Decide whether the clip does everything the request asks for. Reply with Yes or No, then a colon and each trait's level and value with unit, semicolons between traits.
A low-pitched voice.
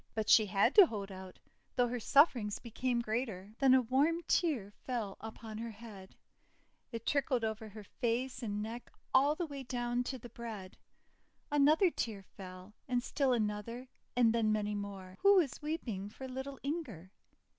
No: high, 235 Hz